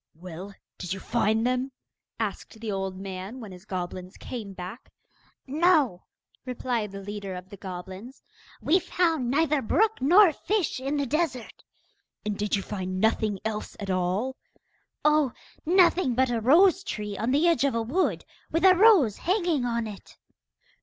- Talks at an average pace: Yes, average, 160 wpm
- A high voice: Yes, high, 235 Hz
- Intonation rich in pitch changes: Yes, wide, 7.3 semitones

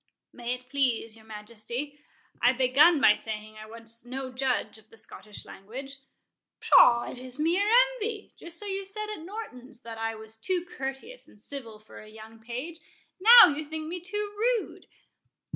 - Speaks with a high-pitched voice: Yes, very high, 260 Hz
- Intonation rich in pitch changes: Yes, wide, 7.4 semitones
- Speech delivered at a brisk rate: No, average, 160 wpm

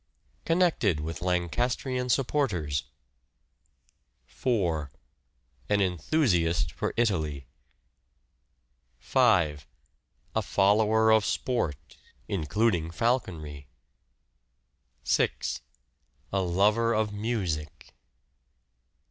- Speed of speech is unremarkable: No, slow, 65 wpm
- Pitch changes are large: Yes, wide, 6.3 semitones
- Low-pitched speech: Yes, low, 100 Hz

